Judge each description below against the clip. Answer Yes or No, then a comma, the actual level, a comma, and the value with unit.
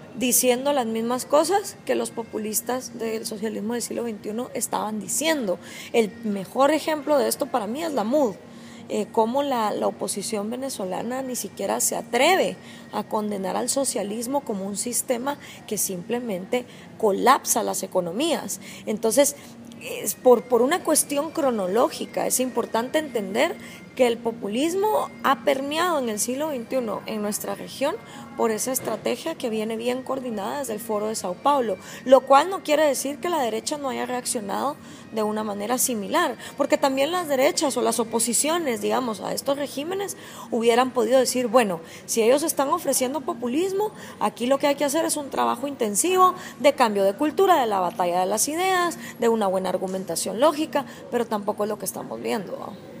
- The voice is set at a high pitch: Yes, very high, 250 Hz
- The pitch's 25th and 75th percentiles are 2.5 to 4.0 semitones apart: No, average, 4.8 semitones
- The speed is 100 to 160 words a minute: No, average, 170 wpm